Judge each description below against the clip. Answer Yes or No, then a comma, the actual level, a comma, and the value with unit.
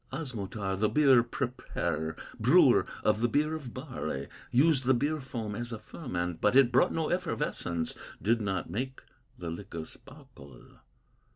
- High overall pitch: No, low, 120 Hz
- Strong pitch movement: Yes, wide, 5.8 semitones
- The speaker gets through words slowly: No, average, 150 wpm